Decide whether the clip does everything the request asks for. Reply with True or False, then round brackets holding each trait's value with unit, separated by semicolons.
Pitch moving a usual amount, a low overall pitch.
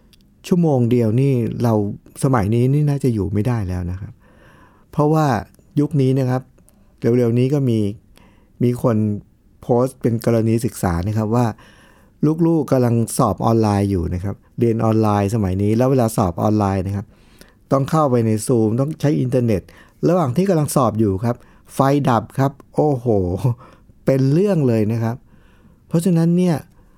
True (4.4 semitones; 115 Hz)